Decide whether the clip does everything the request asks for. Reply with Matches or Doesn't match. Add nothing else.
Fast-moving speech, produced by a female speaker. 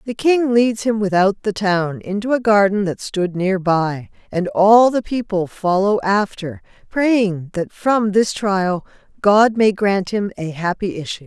Doesn't match